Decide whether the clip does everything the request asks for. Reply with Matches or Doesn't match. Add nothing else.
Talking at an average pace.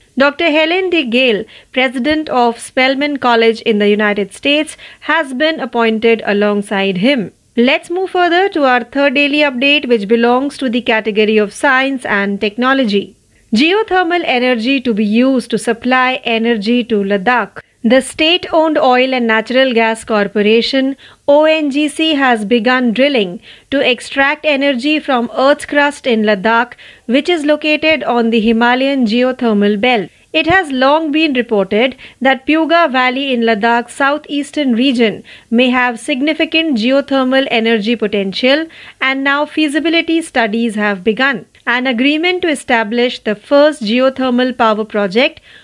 Doesn't match